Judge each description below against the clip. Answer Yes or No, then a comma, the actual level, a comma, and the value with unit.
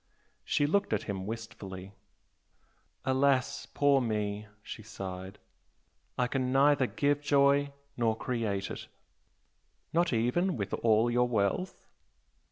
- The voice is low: Yes, low, 120 Hz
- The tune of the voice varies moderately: Yes, average, 5.0 semitones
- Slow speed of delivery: Yes, slow, 115 wpm